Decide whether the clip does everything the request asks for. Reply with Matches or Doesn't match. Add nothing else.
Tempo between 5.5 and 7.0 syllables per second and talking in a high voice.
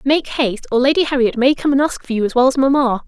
Matches